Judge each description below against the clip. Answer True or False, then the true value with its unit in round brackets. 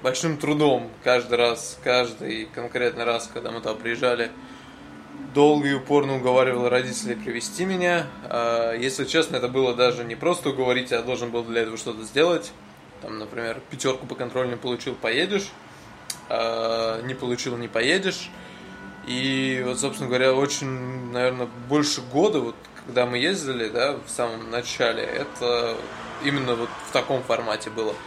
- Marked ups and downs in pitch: False (2.5 semitones)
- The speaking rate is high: False (145 wpm)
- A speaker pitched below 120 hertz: False (125 Hz)